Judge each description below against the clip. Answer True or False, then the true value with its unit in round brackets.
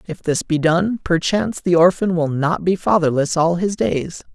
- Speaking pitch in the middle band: True (170 Hz)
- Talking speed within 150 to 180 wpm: False (195 wpm)